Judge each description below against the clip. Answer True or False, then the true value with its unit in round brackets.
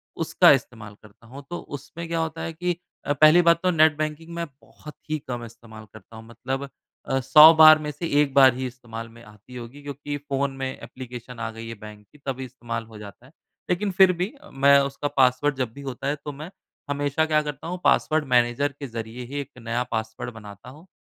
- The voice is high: False (135 Hz)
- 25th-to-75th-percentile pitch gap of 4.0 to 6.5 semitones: True (4.5 semitones)